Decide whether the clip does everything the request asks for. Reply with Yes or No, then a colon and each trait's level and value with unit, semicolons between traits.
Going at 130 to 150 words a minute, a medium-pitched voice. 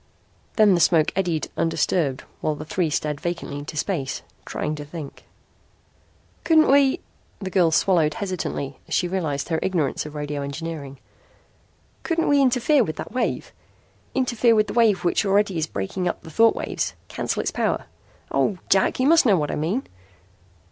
No: average, 170 wpm; medium, 175 Hz